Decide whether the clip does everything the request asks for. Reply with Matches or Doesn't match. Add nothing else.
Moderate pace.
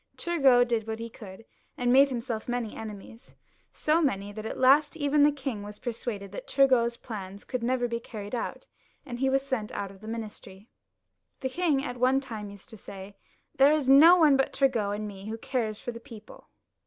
Doesn't match